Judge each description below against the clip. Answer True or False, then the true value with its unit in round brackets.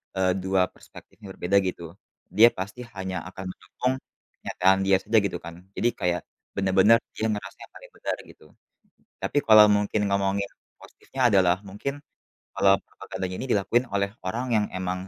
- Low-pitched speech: True (100 Hz)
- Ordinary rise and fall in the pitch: False (2.1 semitones)